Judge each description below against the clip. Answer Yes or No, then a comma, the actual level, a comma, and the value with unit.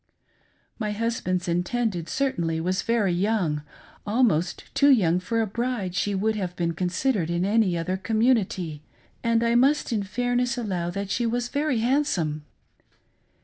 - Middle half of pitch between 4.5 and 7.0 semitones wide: Yes, average, 5.0 semitones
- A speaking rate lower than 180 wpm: Yes, average, 155 wpm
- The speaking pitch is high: Yes, high, 205 Hz